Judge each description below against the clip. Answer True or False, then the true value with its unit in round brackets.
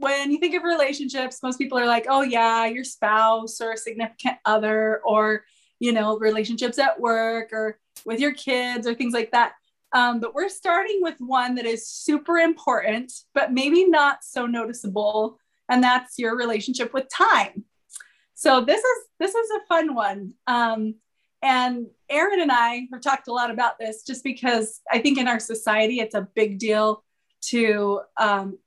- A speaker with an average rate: True (175 wpm)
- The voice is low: False (240 Hz)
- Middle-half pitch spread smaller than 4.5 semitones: True (3.5 semitones)